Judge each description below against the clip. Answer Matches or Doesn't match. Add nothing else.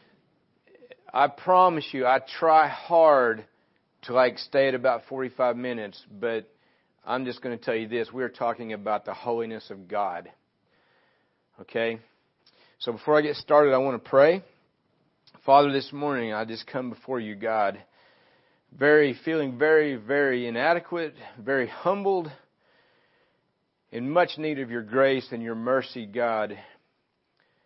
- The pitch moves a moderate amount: Matches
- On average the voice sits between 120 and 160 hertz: Matches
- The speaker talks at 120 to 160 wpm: Matches